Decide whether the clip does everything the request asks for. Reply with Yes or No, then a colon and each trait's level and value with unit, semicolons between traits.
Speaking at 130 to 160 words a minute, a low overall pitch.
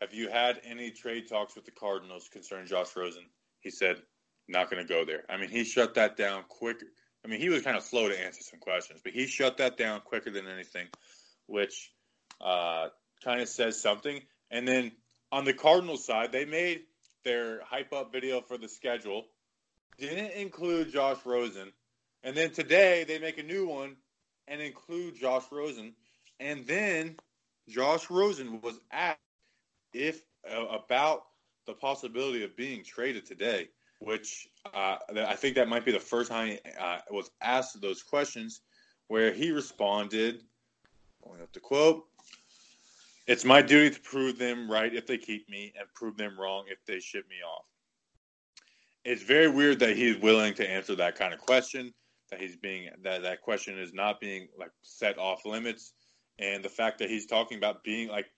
No: average, 180 wpm; low, 120 Hz